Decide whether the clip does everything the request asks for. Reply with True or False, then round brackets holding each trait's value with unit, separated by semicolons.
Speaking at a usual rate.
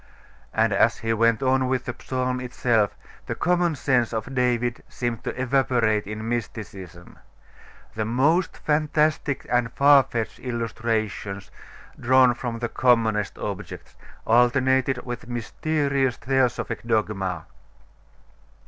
False (115 wpm)